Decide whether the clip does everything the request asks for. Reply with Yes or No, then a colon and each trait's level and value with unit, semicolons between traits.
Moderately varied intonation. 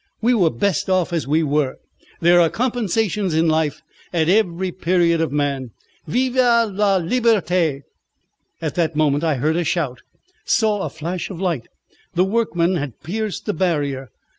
Yes: average, 4.5 semitones